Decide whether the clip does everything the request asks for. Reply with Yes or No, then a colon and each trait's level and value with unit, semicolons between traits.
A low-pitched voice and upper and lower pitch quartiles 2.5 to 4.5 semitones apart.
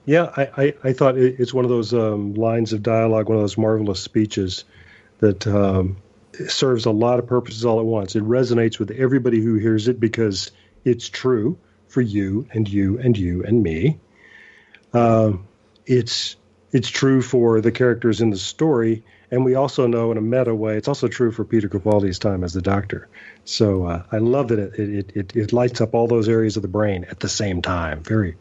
Yes: low, 110 Hz; average, 2.8 semitones